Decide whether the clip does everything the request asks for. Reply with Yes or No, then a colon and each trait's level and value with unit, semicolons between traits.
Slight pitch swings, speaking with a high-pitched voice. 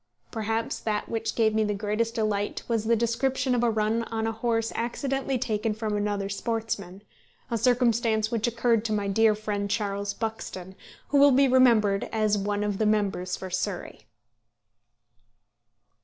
Yes: narrow, 2.0 semitones; high, 220 Hz